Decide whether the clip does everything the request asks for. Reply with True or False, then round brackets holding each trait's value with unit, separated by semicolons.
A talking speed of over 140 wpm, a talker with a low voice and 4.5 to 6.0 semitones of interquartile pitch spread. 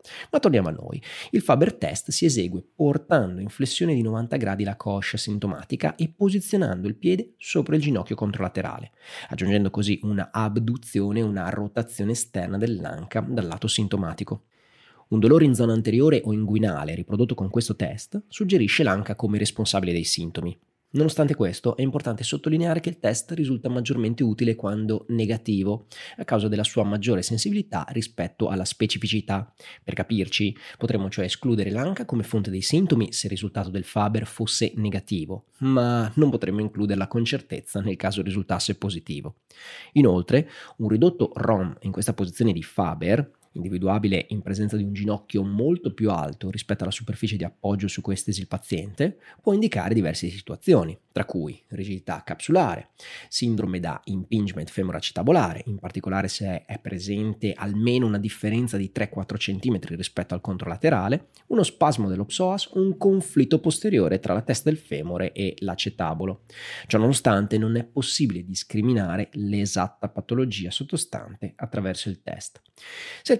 False (150 wpm; 105 Hz; 3.5 semitones)